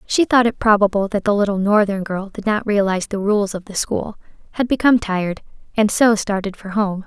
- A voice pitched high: Yes, high, 205 Hz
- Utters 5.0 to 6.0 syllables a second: Yes, 5.6 syllables/s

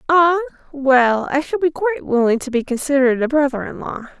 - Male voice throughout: No, female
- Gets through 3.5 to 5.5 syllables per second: No, 5.8 syllables/s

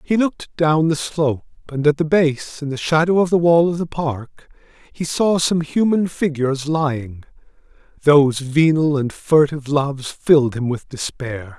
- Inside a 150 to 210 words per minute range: Yes, average, 170 wpm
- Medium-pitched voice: Yes, medium, 150 Hz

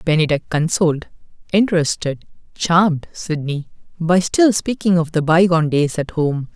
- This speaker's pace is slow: Yes, slow, 130 wpm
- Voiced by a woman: No, male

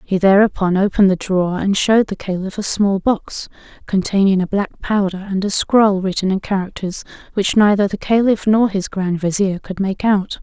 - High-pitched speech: Yes, high, 195 Hz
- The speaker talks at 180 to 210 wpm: Yes, average, 190 wpm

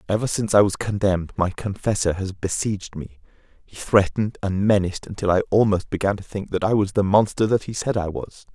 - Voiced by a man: Yes, male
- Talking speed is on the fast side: Yes, fast, 210 wpm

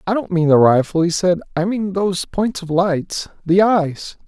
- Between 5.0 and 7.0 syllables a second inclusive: No, 4.5 syllables/s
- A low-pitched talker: No, medium, 180 Hz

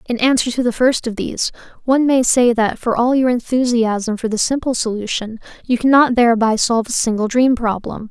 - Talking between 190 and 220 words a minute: Yes, average, 200 wpm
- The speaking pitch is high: Yes, high, 235 Hz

